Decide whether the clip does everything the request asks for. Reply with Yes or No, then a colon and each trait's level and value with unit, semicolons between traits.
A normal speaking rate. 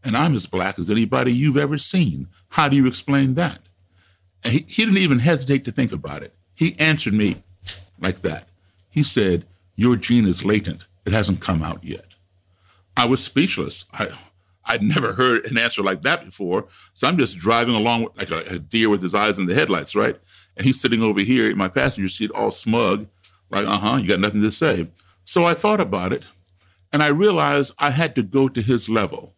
No: fast, 210 wpm